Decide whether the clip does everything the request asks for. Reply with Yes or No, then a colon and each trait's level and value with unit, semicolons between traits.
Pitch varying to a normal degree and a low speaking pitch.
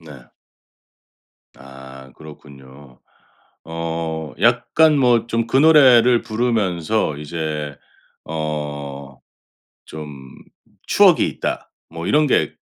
No: wide, 8.2 semitones; very low, 80 Hz